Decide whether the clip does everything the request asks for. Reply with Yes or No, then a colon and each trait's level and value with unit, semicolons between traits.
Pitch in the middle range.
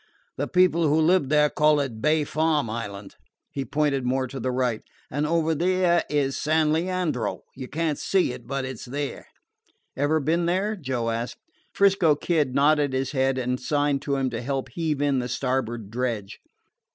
Yes: medium, 145 Hz